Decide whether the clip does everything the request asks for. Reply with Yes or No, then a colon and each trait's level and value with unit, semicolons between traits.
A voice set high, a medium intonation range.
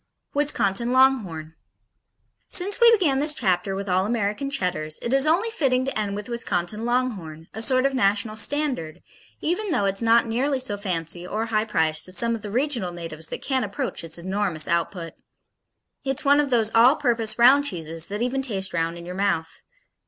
No: high, 220 Hz; wide, 6.6 semitones